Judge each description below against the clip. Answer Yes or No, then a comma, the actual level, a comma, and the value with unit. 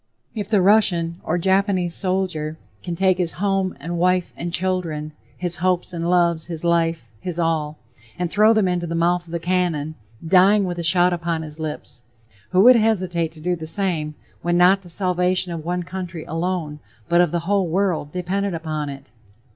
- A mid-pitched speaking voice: Yes, medium, 175 Hz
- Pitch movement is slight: Yes, narrow, 2.0 semitones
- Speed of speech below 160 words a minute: No, average, 185 wpm